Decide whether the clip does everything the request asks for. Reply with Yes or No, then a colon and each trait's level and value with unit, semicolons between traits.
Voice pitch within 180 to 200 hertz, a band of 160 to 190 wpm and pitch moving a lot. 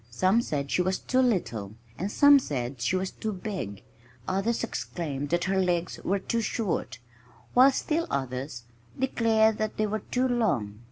Yes: high, 190 Hz; average, 165 wpm; wide, 8.5 semitones